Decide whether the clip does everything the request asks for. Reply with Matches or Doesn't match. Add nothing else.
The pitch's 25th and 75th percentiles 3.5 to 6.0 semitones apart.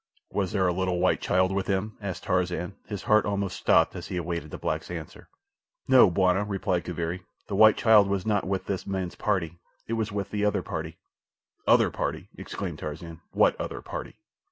Doesn't match